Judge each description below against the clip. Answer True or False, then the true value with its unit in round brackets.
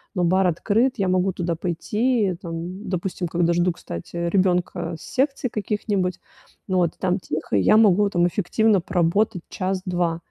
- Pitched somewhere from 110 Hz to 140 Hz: False (185 Hz)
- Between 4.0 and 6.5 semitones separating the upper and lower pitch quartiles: False (2.7 semitones)